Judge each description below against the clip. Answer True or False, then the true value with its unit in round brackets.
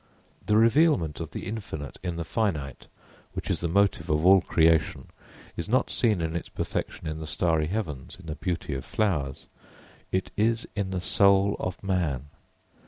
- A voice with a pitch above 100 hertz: False (90 Hz)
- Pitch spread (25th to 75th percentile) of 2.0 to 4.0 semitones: False (4.4 semitones)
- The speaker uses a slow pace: False (170 wpm)